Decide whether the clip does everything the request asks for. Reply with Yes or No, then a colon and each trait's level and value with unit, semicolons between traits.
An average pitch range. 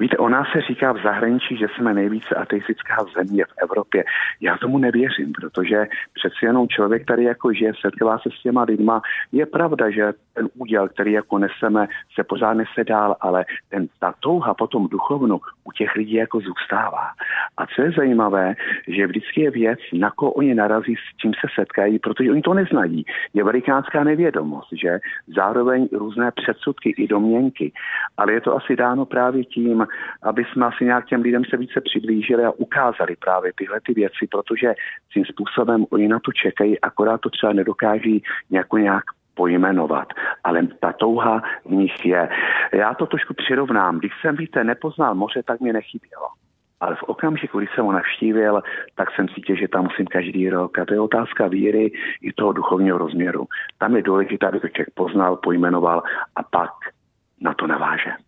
Yes: average, 3.5 semitones